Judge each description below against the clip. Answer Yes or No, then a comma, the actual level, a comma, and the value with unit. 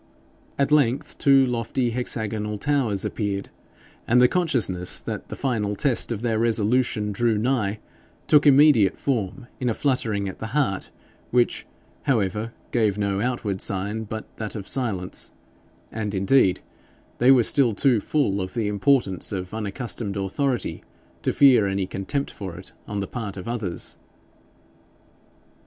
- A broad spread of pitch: No, average, 4.2 semitones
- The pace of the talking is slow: No, average, 145 wpm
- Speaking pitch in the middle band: No, low, 110 Hz